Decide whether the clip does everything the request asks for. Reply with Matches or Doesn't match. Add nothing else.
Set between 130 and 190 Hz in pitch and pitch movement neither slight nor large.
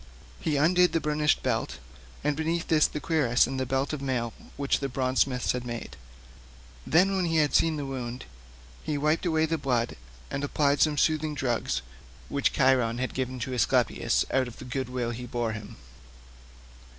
Matches